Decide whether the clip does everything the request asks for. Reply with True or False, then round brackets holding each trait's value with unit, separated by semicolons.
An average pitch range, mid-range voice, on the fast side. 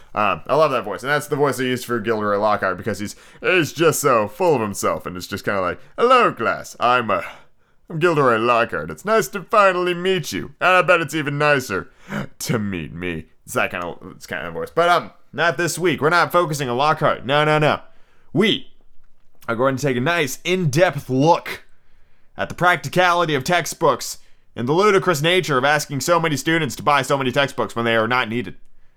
False (6.4 semitones; 145 Hz; 215 wpm)